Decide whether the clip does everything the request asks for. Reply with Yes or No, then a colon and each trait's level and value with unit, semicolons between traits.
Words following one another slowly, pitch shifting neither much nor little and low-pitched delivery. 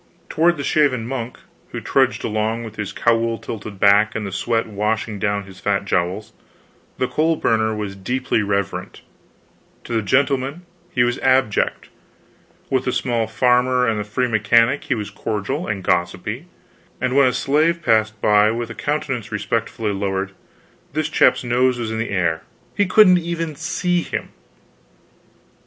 No: average, 160 wpm; average, 4.0 semitones; low, 115 Hz